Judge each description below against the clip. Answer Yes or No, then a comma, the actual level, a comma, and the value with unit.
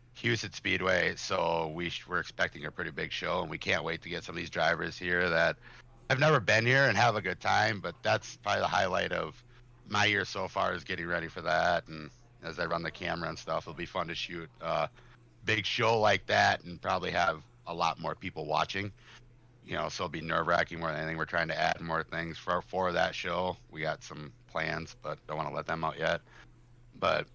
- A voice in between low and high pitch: No, very low, 90 Hz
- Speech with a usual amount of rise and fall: No, wide, 6.1 semitones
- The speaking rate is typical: No, fast, 230 wpm